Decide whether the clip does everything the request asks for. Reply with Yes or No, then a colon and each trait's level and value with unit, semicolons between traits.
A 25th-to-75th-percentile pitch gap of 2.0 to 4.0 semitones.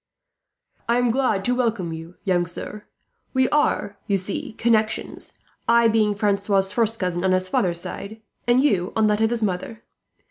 Yes: average, 3.6 semitones